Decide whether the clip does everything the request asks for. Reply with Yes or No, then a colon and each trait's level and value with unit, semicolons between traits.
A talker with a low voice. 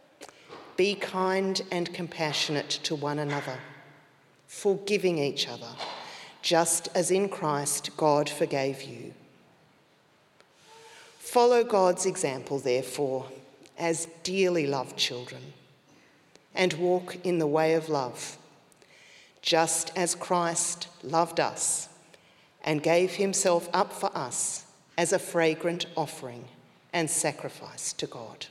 No: medium, 165 Hz